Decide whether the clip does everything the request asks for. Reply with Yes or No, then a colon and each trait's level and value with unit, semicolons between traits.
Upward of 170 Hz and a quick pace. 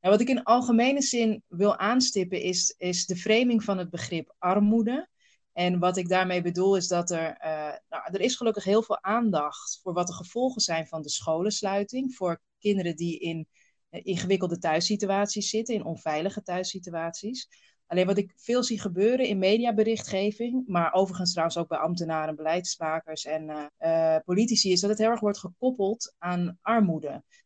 No: high, 190 Hz; average, 175 wpm